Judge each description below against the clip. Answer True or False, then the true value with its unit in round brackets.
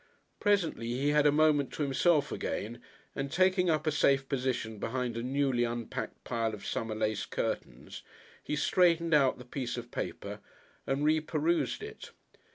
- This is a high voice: False (140 Hz)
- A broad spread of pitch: False (4.4 semitones)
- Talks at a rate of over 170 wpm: False (160 wpm)